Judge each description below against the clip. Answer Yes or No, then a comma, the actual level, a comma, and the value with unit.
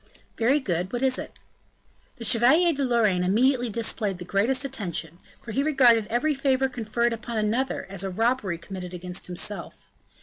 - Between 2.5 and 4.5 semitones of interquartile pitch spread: No, average, 5.2 semitones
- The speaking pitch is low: No, high, 230 Hz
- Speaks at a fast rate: No, average, 165 wpm